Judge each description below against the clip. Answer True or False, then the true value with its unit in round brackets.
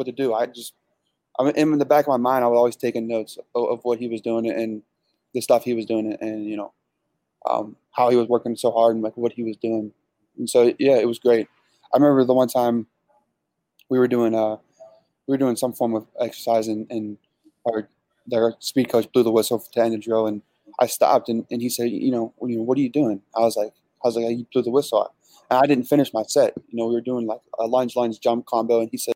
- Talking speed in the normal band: False (255 wpm)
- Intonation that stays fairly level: True (1.9 semitones)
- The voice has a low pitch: True (120 Hz)